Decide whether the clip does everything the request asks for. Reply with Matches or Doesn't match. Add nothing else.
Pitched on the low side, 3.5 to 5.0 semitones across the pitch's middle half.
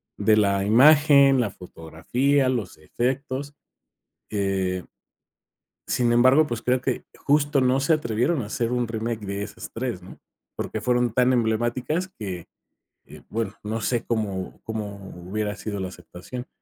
Matches